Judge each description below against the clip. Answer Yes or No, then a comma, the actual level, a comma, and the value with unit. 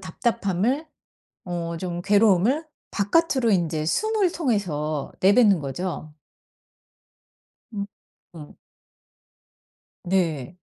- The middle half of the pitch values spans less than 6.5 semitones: Yes, wide, 5.6 semitones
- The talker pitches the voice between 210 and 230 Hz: No, high, 190 Hz